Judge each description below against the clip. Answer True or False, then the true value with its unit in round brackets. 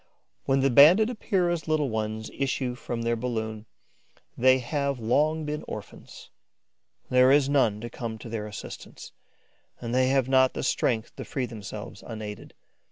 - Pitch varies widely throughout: False (3.8 semitones)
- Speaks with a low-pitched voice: True (125 Hz)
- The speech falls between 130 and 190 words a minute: True (155 wpm)